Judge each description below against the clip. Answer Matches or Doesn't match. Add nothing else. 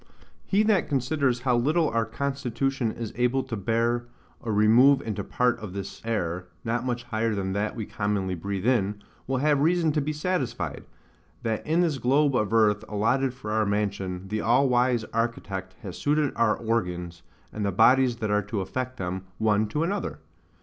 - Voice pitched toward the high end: Doesn't match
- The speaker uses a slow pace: Doesn't match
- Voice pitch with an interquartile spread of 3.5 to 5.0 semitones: Matches